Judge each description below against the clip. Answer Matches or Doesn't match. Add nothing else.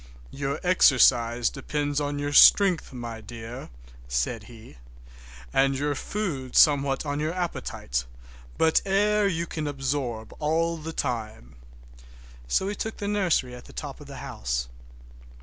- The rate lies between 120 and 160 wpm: Matches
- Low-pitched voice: Doesn't match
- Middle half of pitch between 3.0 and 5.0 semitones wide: Doesn't match